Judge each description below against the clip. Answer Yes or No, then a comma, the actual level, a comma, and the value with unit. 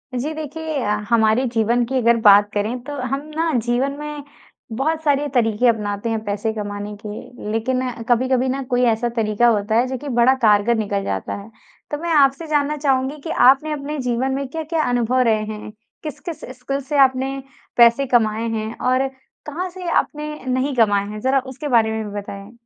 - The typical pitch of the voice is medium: No, very high, 250 Hz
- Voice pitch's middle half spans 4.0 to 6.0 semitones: Yes, average, 4.3 semitones